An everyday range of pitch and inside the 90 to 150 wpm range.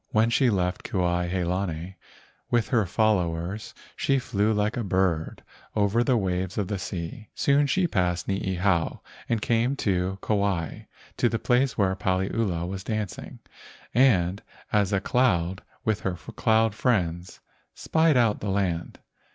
Yes: average, 3.8 semitones; average, 145 wpm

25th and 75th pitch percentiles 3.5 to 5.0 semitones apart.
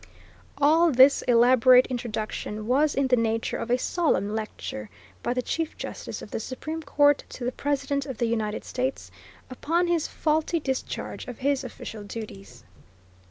Yes: average, 3.8 semitones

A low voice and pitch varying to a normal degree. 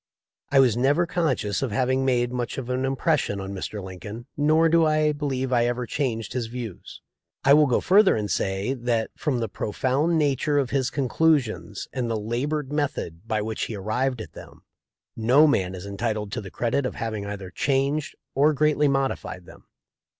Yes: low, 125 Hz; average, 4.7 semitones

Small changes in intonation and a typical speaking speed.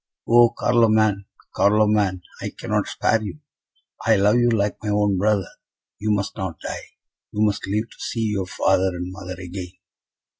Yes: narrow, 2.3 semitones; average, 160 wpm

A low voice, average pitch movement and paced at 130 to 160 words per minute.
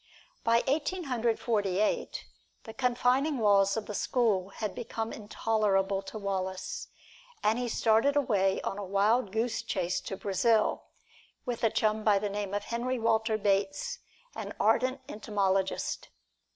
No: high, 215 Hz; average, 3.2 semitones; average, 145 wpm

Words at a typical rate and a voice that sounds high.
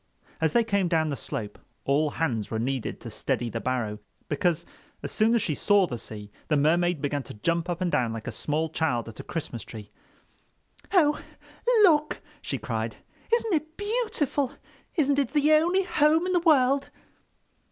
No: average, 180 wpm; medium, 170 Hz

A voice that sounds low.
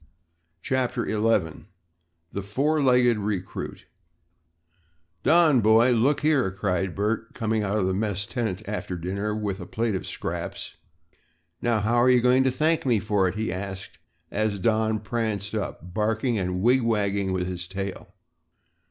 Yes: low, 110 Hz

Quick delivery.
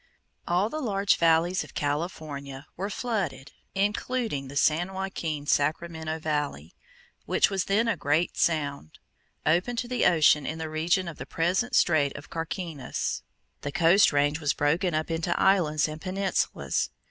No: average, 150 wpm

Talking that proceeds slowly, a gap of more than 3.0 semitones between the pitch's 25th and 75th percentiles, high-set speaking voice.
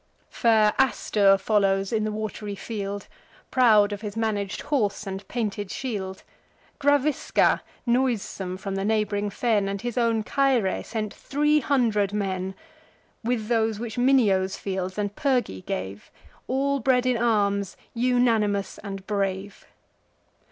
Yes: slow, 130 wpm; average, 3.5 semitones; high, 210 Hz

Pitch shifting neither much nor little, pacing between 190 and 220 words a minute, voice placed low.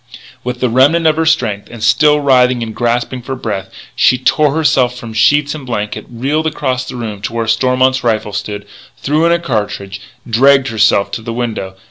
Yes: average, 3.9 semitones; average, 195 wpm; low, 125 Hz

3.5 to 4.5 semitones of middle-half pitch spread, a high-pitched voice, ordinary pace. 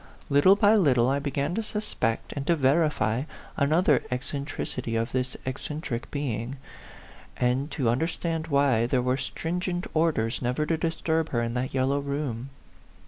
No: average, 4.2 semitones; medium, 140 Hz; average, 155 wpm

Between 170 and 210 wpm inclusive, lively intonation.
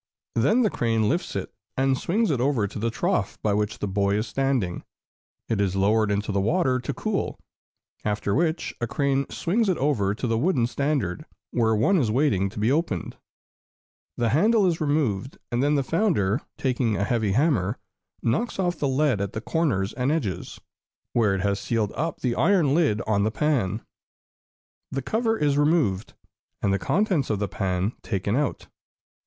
Yes: average, 180 wpm; wide, 6.5 semitones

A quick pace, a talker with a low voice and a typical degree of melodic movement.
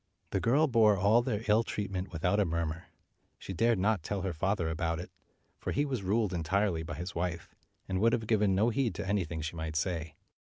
Yes: fast, 210 wpm; very low, 95 Hz; average, 4.4 semitones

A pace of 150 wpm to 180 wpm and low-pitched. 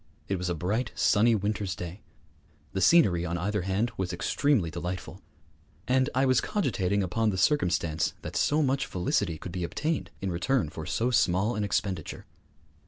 Yes: average, 170 wpm; very low, 95 Hz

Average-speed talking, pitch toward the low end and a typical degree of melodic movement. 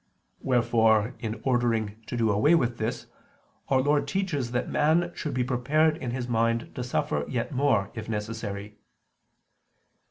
Yes: average, 150 wpm; low, 120 Hz; average, 3.5 semitones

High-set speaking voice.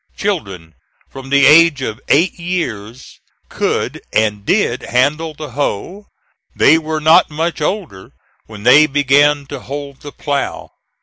No: medium, 145 Hz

